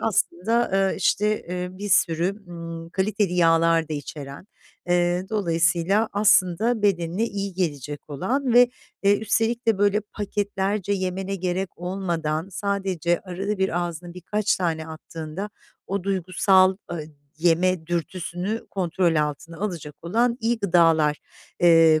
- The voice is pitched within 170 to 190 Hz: Yes, medium, 185 Hz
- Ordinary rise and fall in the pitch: Yes, average, 3.3 semitones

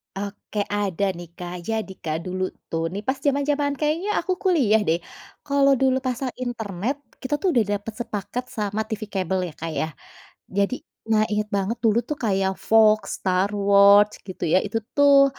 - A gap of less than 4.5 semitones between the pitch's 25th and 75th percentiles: No, average, 5.1 semitones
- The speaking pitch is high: Yes, high, 210 Hz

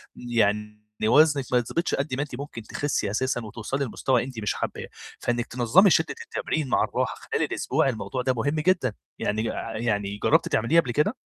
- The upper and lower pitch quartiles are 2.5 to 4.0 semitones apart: No, average, 4.4 semitones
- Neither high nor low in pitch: No, low, 125 Hz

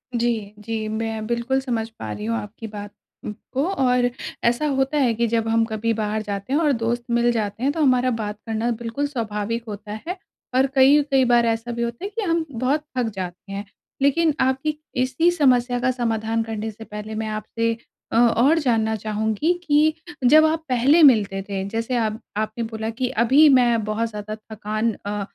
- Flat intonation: No, average, 3.3 semitones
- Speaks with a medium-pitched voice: No, high, 230 Hz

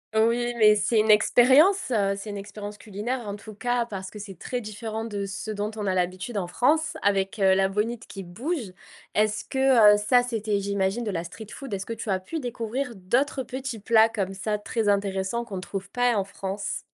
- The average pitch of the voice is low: No, high, 210 Hz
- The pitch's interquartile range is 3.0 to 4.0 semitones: Yes, average, 3.3 semitones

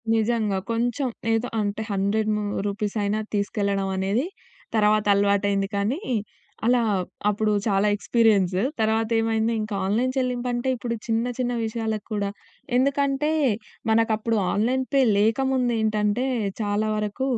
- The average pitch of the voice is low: No, high, 220 Hz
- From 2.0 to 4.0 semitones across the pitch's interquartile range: Yes, average, 2.8 semitones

